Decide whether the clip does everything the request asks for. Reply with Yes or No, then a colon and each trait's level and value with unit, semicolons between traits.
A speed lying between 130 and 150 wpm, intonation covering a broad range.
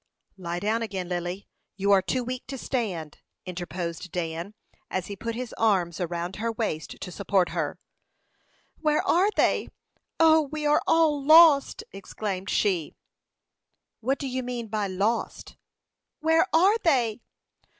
Yes: average, 140 wpm; wide, 6.9 semitones